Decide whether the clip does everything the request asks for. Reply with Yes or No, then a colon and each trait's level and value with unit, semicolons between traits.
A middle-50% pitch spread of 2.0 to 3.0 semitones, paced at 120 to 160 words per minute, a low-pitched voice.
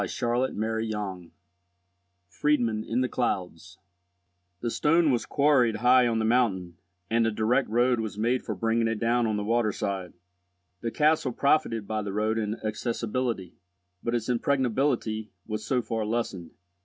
Yes: narrow, 2.5 semitones; average, 155 wpm; low, 115 Hz